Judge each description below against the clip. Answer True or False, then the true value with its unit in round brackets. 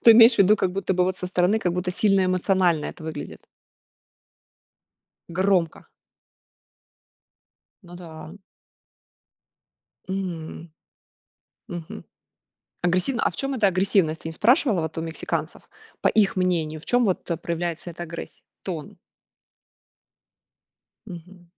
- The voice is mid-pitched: True (180 Hz)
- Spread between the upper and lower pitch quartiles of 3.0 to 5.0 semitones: False (2.6 semitones)